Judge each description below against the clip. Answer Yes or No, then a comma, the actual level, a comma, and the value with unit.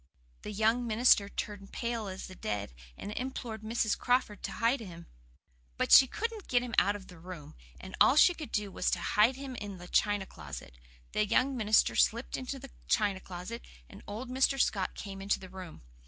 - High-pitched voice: Yes, high, 210 Hz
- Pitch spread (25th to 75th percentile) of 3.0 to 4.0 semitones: No, average, 4.5 semitones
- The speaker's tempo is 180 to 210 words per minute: Yes, average, 200 wpm